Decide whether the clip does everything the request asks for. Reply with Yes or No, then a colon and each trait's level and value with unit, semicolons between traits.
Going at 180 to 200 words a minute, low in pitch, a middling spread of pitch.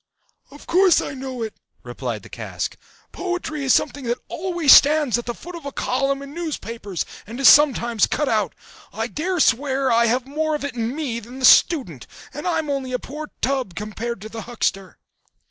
No: average, 195 wpm; very high, 265 Hz; average, 4.4 semitones